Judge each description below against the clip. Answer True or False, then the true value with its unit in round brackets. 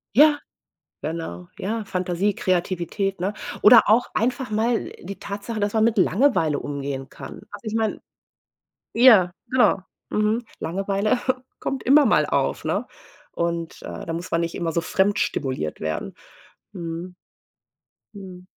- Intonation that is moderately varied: True (4.6 semitones)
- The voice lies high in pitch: True (195 Hz)